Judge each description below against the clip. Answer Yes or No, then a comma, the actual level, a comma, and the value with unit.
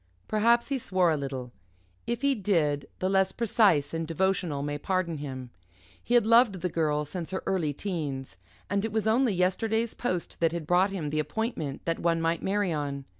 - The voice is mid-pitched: Yes, medium, 180 Hz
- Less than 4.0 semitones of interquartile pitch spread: No, wide, 5.6 semitones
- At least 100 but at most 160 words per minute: No, average, 190 wpm